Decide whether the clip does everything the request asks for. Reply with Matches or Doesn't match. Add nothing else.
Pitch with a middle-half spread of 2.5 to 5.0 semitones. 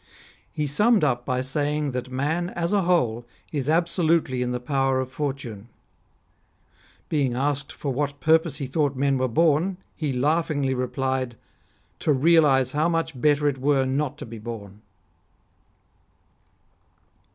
Matches